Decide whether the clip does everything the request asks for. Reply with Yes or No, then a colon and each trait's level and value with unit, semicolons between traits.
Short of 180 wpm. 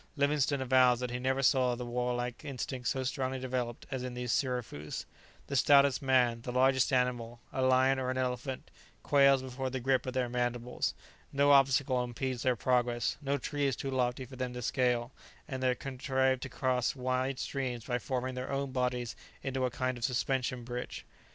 No: average, 185 wpm